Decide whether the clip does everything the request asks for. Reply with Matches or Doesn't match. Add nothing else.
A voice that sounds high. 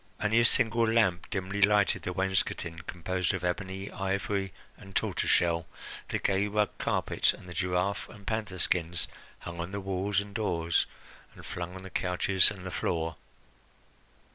Doesn't match